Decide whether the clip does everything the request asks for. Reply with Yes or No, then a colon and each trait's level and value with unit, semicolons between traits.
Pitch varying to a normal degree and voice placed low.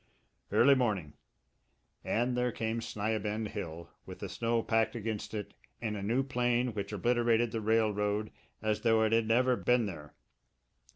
No: narrow, 2.2 semitones; low, 110 Hz